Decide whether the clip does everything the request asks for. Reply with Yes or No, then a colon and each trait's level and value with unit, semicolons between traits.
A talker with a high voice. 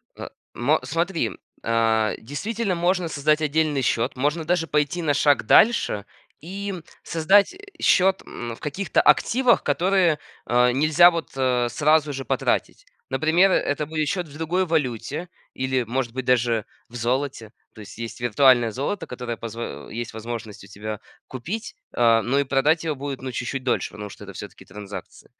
No: medium, 140 Hz